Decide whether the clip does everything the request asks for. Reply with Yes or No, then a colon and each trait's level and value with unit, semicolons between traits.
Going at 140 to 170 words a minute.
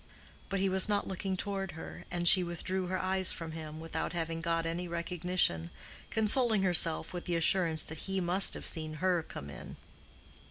No: average, 185 wpm